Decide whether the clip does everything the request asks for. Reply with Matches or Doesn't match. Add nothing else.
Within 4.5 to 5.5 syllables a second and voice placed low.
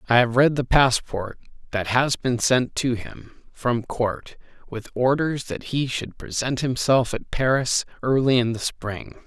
Doesn't match